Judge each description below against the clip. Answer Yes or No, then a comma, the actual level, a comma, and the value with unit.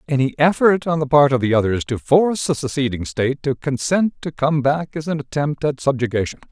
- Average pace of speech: No, fast, 210 wpm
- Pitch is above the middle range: No, medium, 140 Hz